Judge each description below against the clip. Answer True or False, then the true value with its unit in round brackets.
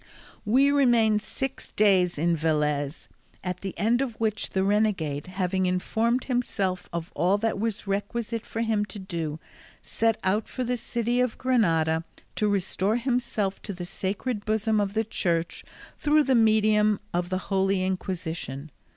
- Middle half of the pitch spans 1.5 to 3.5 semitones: False (3.9 semitones)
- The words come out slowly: False (155 wpm)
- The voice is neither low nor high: False (205 Hz)